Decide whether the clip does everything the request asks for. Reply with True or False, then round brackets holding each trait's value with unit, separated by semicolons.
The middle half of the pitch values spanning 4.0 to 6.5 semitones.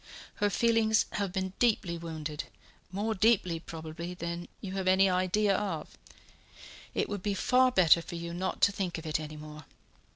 False (3.4 semitones)